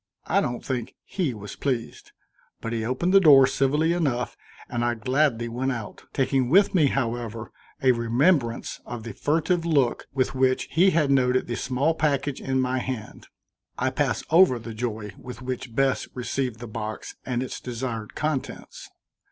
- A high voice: No, low, 130 Hz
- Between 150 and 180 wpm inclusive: Yes, average, 170 wpm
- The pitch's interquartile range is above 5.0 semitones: No, average, 3.2 semitones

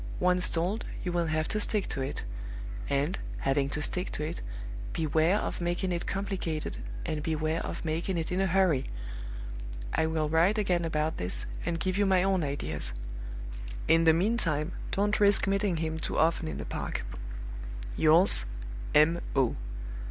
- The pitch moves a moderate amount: Yes, average, 3.3 semitones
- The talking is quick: No, average, 165 wpm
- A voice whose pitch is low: No, medium, 165 Hz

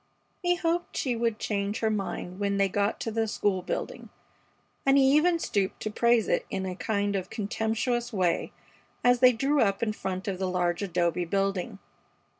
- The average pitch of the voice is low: No, high, 210 Hz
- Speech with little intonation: No, average, 3.7 semitones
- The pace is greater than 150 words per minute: Yes, average, 185 wpm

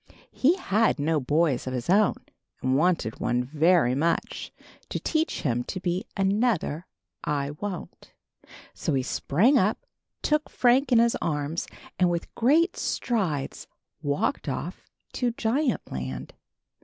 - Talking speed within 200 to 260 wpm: No, slow, 135 wpm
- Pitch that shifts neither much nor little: No, wide, 8.6 semitones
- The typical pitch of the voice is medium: Yes, medium, 175 Hz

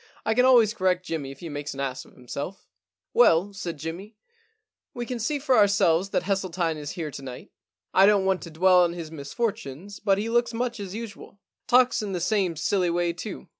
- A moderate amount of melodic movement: Yes, average, 4.8 semitones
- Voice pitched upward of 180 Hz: Yes, high, 190 Hz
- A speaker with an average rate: No, fast, 225 wpm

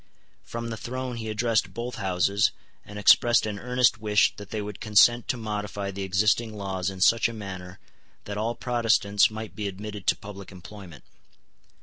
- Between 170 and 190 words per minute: Yes, average, 175 wpm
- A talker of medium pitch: No, low, 105 Hz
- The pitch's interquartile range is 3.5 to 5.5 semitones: No, average, 2.7 semitones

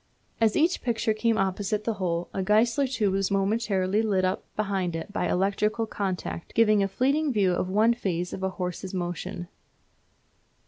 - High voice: Yes, high, 200 Hz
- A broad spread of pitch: No, average, 3.1 semitones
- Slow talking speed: No, average, 170 wpm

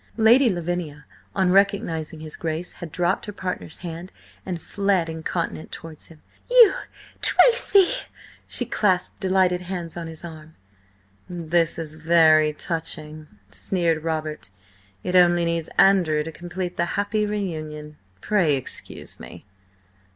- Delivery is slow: Yes, slow, 130 wpm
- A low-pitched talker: No, medium, 170 Hz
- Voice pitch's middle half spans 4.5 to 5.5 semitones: No, average, 3.1 semitones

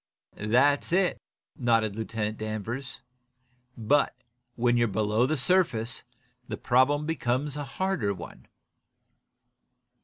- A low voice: Yes, low, 120 Hz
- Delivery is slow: Yes, slow, 100 wpm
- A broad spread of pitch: No, average, 4.8 semitones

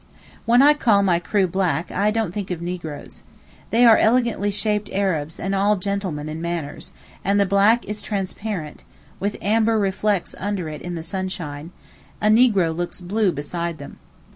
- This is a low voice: No, high, 195 Hz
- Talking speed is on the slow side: No, average, 165 wpm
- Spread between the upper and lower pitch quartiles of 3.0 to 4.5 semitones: Yes, average, 3.6 semitones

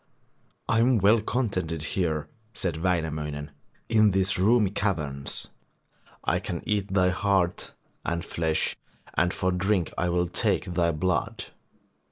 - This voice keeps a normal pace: No, slow, 130 wpm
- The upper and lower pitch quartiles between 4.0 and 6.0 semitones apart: No, average, 3.3 semitones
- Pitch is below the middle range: Yes, very low, 90 Hz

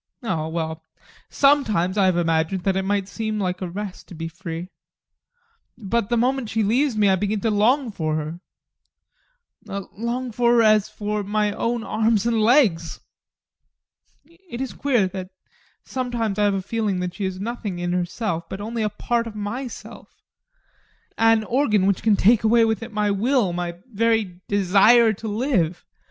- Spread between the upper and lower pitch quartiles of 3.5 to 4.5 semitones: Yes, average, 3.8 semitones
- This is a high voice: Yes, high, 210 Hz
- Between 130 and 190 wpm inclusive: Yes, average, 170 wpm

